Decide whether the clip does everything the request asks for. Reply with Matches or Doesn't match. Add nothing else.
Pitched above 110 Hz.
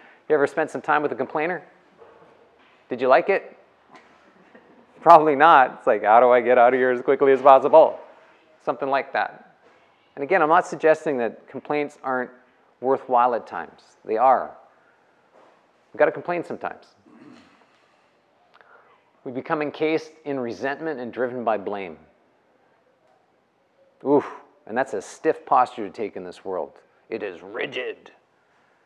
Matches